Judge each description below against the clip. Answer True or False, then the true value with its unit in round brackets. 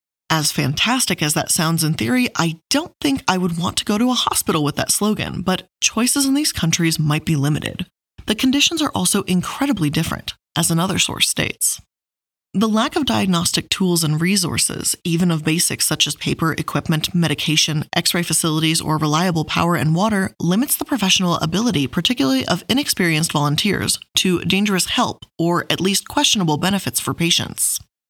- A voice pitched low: False (170 Hz)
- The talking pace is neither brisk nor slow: True (170 wpm)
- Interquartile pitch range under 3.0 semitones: False (4.0 semitones)